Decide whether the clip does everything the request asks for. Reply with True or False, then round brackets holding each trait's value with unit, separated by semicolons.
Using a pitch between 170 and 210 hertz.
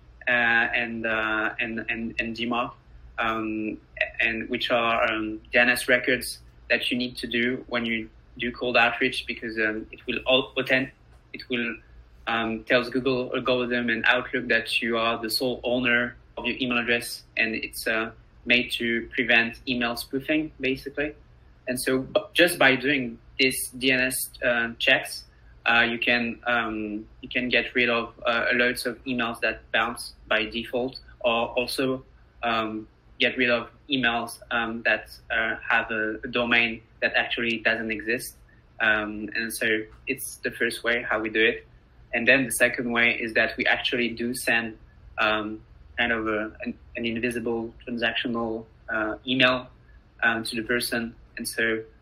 False (120 Hz)